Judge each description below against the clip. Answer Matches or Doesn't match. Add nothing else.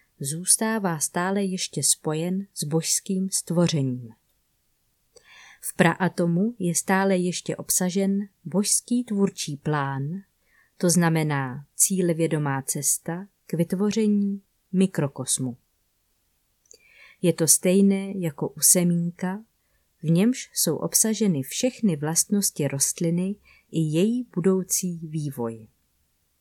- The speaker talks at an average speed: Doesn't match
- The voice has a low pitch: Doesn't match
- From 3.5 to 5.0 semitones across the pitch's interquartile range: Matches